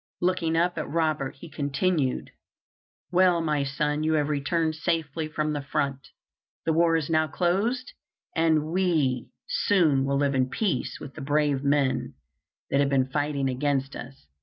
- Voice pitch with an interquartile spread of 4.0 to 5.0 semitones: No, average, 3.0 semitones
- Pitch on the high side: No, medium, 150 Hz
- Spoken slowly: No, average, 160 wpm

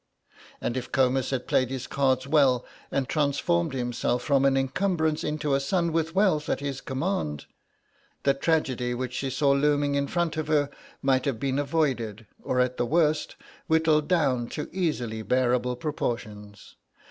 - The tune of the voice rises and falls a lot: No, average, 3.4 semitones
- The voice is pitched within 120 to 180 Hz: Yes, medium, 140 Hz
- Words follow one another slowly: No, average, 160 wpm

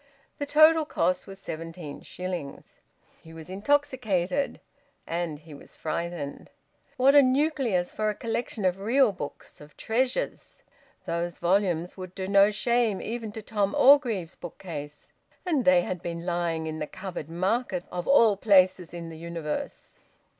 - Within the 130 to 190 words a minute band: Yes, average, 145 wpm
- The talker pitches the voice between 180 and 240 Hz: Yes, medium, 185 Hz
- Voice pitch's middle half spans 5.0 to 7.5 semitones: Yes, wide, 5.5 semitones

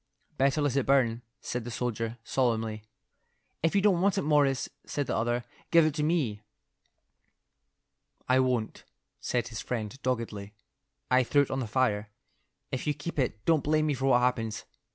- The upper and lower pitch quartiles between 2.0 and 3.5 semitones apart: No, average, 4.2 semitones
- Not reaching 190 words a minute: Yes, average, 175 wpm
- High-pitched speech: No, low, 130 Hz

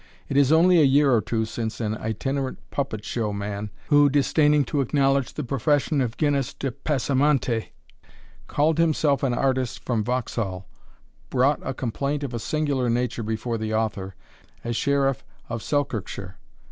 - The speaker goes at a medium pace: Yes, average, 155 wpm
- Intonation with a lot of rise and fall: No, average, 4.1 semitones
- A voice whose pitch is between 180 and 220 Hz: No, low, 130 Hz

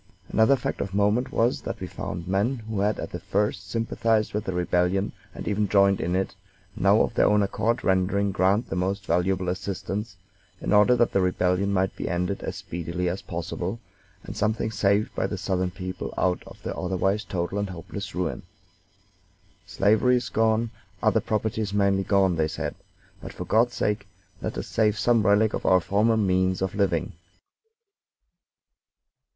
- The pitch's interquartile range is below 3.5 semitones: Yes, narrow, 2.5 semitones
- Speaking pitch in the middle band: No, low, 100 Hz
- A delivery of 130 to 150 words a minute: No, average, 175 wpm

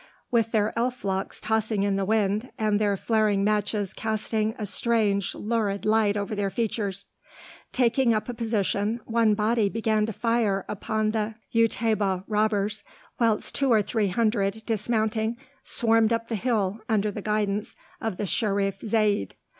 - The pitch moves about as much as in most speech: No, narrow, 1.9 semitones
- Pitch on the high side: Yes, high, 215 Hz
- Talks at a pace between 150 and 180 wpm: Yes, average, 155 wpm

